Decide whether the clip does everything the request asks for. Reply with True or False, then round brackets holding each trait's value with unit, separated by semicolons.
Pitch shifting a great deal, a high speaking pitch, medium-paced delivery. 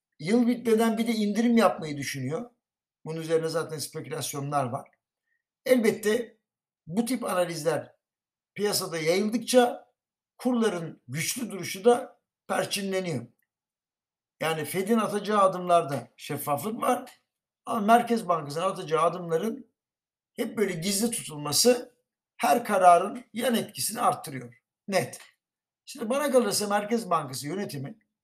True (6.6 semitones; 200 Hz; 110 wpm)